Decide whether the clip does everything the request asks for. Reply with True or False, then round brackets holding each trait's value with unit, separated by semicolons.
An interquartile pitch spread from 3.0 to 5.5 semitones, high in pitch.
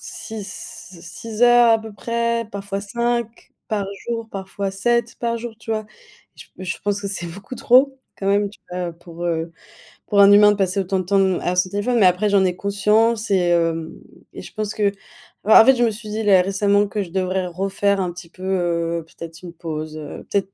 True (3.4 semitones; 200 Hz)